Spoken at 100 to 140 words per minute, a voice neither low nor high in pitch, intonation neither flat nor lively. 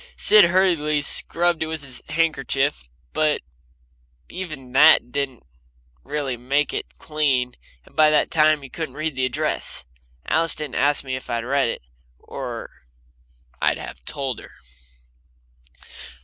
Yes: slow, 135 wpm; medium, 145 Hz; average, 3.1 semitones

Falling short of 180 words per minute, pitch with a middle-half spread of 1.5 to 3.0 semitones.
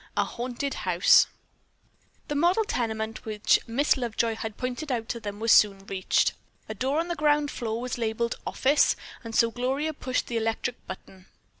No: average, 170 wpm; average, 3.7 semitones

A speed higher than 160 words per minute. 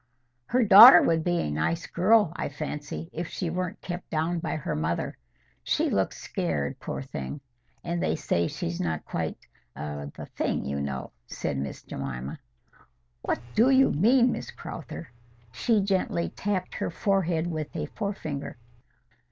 No: average, 150 wpm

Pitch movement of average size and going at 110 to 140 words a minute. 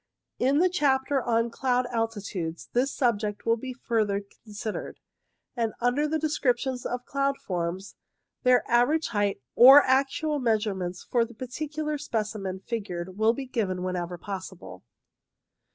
Yes: average, 4.7 semitones; slow, 135 wpm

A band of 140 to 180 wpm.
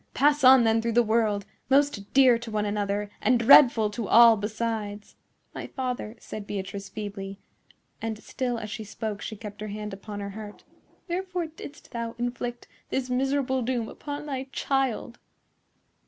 Yes: average, 155 wpm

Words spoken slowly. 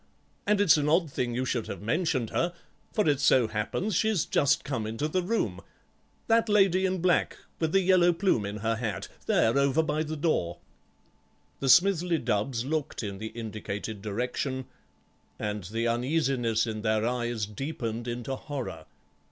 No: average, 165 wpm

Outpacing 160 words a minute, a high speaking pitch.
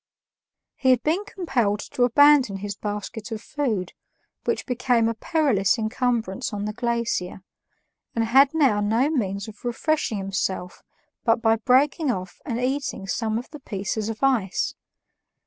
No: average, 145 wpm; high, 230 Hz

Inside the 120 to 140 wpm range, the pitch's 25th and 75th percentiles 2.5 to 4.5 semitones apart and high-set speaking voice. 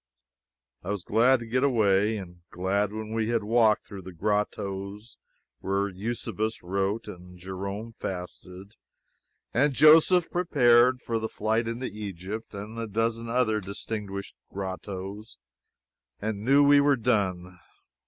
No: slow, 135 wpm; average, 3.0 semitones; low, 105 Hz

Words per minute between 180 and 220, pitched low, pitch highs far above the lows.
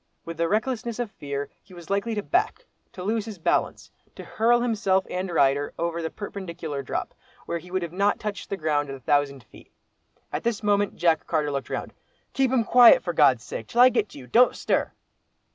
No: average, 195 wpm; high, 190 Hz; wide, 6.0 semitones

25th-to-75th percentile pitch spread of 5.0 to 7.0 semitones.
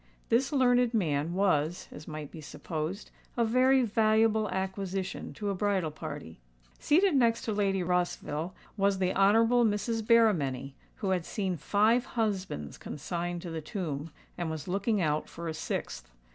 Yes: wide, 5.5 semitones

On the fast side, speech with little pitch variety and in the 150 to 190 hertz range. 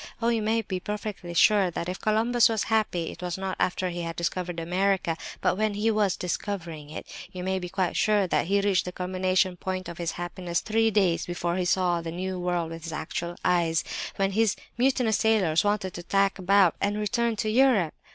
No: fast, 210 wpm; average, 3.2 semitones; medium, 185 Hz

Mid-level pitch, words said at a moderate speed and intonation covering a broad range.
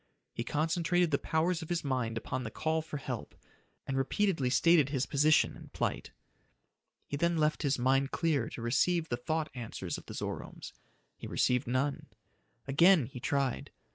No: medium, 145 Hz; average, 170 wpm; average, 3.9 semitones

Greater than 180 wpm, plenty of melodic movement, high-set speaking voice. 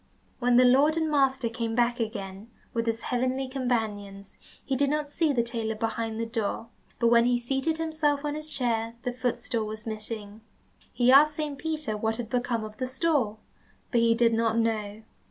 No: average, 190 wpm; average, 3.1 semitones; high, 240 Hz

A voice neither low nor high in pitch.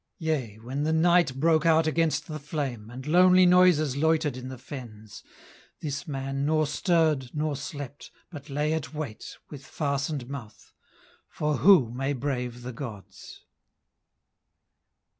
Yes: medium, 145 Hz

